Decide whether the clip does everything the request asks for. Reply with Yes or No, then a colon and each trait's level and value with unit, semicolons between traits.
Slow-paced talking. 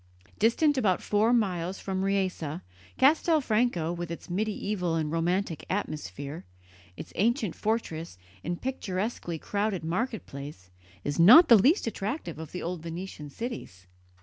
Yes: slow, 130 wpm